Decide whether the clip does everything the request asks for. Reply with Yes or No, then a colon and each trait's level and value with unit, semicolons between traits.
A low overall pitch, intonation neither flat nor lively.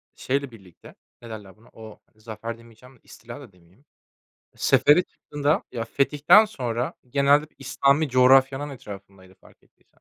Yes: low, 125 Hz; average, 4.2 semitones